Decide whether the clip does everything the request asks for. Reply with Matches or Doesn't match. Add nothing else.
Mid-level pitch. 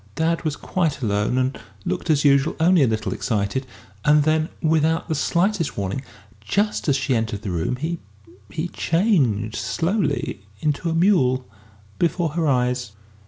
Matches